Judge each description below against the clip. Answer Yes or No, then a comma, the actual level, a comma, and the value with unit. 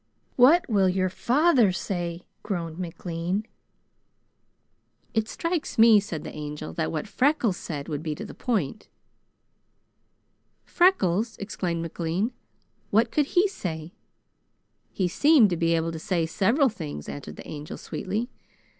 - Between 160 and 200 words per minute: No, slow, 135 wpm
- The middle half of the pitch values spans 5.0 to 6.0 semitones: Yes, wide, 5.5 semitones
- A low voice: No, medium, 185 Hz